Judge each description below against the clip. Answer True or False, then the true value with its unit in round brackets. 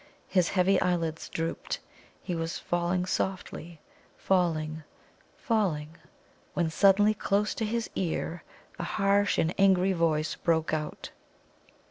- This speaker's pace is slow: True (115 wpm)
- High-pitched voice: False (175 Hz)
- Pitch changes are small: False (3.1 semitones)